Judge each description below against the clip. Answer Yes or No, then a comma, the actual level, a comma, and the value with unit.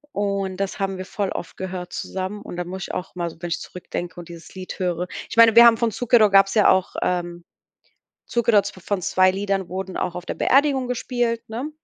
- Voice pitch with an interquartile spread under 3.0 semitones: No, average, 3.7 semitones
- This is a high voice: Yes, high, 195 Hz